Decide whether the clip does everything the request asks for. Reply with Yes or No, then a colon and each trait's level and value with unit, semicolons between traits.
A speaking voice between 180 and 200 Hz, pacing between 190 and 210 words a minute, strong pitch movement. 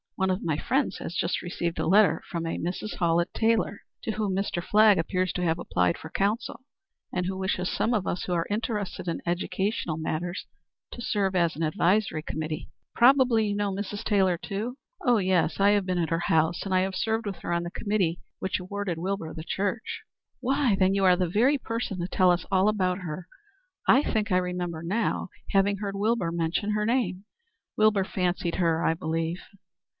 No: high, 190 Hz; average, 195 wpm; average, 3.3 semitones